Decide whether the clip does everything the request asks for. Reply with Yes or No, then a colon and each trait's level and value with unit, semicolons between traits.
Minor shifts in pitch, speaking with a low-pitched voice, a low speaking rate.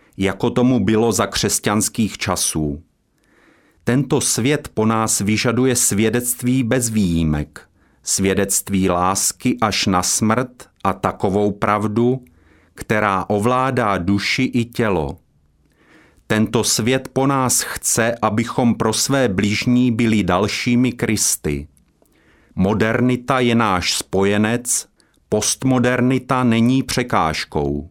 No: average, 3.9 semitones; low, 110 Hz; slow, 100 wpm